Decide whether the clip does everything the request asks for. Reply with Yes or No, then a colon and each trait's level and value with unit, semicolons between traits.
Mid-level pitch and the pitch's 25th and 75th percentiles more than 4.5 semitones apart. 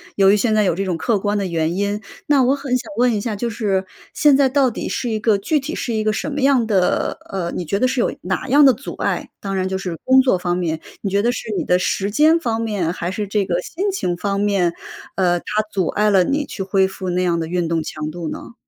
No: high, 205 Hz; average, 5.2 semitones